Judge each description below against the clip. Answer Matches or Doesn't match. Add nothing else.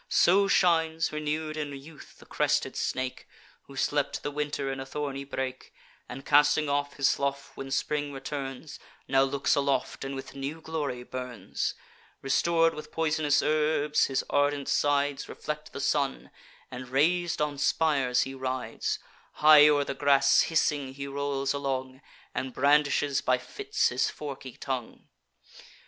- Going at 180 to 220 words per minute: Doesn't match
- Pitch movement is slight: Matches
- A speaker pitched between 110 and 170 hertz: Matches